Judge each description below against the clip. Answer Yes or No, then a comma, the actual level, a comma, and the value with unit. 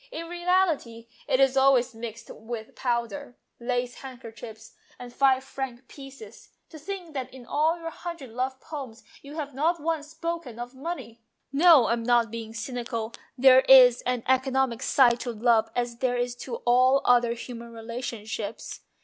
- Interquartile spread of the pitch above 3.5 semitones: No, average, 2.8 semitones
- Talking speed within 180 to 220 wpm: No, average, 165 wpm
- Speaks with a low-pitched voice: No, very high, 250 Hz